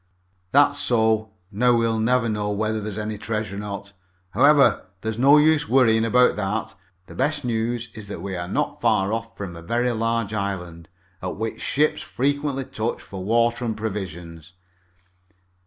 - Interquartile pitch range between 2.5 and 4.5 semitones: Yes, average, 3.2 semitones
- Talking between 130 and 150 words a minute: No, average, 170 wpm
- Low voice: Yes, low, 110 Hz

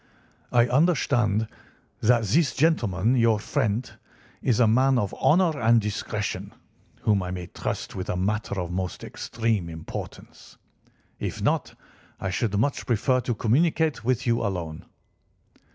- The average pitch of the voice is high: No, low, 115 Hz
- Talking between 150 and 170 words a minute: No, average, 140 wpm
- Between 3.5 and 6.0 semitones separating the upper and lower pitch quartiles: Yes, average, 4.3 semitones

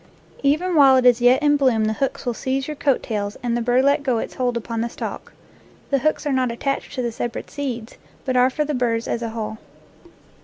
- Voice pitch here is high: Yes, very high, 250 Hz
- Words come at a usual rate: No, fast, 235 wpm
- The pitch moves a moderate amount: Yes, average, 3.0 semitones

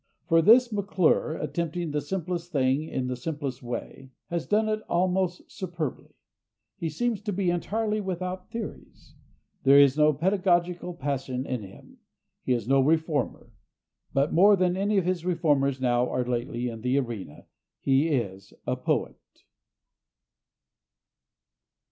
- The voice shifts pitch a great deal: Yes, wide, 5.7 semitones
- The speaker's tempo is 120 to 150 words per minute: Yes, average, 140 wpm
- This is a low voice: No, medium, 160 Hz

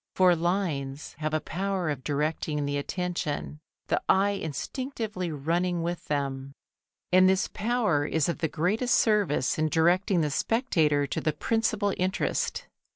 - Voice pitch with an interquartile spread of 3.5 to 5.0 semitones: Yes, average, 4.6 semitones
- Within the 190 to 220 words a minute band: No, average, 145 wpm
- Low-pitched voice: No, medium, 170 Hz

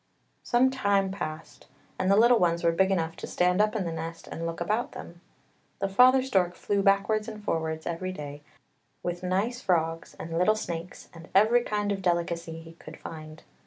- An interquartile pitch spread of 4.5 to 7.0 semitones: No, average, 3.8 semitones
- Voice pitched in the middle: Yes, medium, 180 Hz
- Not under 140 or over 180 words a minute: No, average, 190 wpm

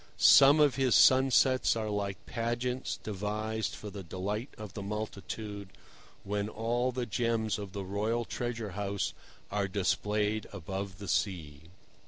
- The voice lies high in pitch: No, low, 105 Hz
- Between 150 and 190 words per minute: No, average, 140 wpm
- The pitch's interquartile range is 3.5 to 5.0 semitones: No, average, 2.7 semitones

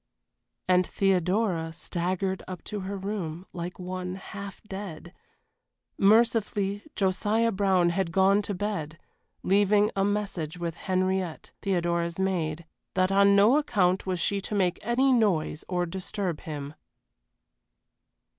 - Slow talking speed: Yes, slow, 125 wpm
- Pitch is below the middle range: No, high, 190 Hz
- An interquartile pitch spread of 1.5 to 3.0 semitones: Yes, narrow, 2.5 semitones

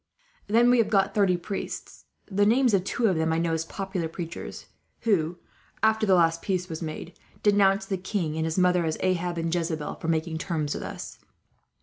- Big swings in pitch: No, average, 3.5 semitones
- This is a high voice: No, medium, 180 Hz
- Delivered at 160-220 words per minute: Yes, average, 200 wpm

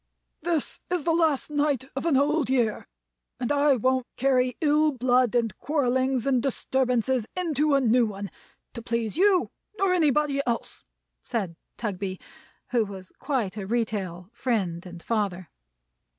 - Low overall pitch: No, very high, 255 Hz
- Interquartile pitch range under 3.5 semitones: No, average, 5.0 semitones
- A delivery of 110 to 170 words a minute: Yes, average, 145 wpm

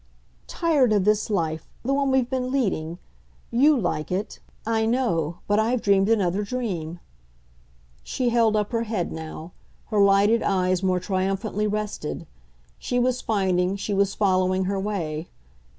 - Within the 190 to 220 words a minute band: No, average, 150 wpm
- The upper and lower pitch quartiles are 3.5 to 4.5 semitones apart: Yes, average, 3.9 semitones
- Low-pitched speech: No, high, 205 Hz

